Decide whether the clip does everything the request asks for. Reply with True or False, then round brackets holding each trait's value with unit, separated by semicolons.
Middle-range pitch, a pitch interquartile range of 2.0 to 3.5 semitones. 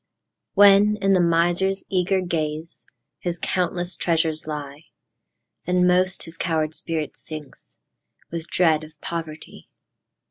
True (170 Hz; 2.6 semitones)